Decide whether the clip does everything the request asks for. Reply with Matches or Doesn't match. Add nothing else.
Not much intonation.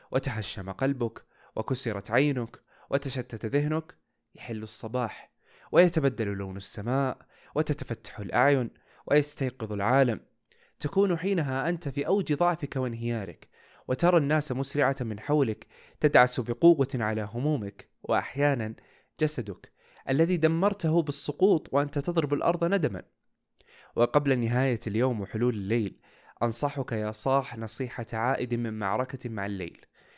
Doesn't match